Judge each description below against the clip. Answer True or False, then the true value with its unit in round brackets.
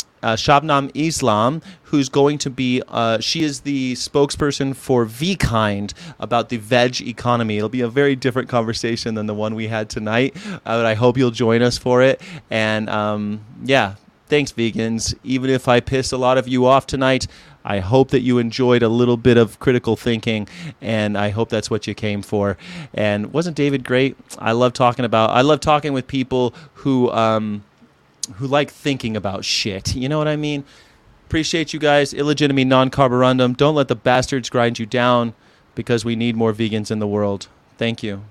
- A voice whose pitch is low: True (125 Hz)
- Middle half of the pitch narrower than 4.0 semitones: True (3.5 semitones)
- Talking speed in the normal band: True (190 wpm)